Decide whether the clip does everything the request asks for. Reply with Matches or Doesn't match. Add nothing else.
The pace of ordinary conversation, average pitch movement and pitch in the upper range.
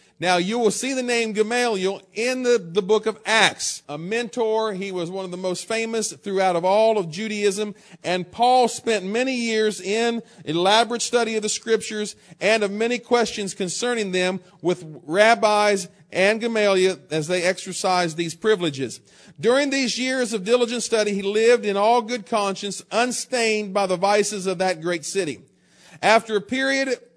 Matches